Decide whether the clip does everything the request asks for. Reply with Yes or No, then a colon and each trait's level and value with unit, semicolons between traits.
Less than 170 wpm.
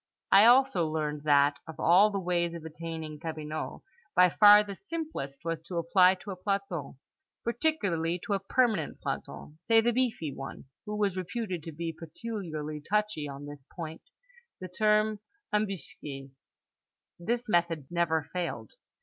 Yes: average, 150 wpm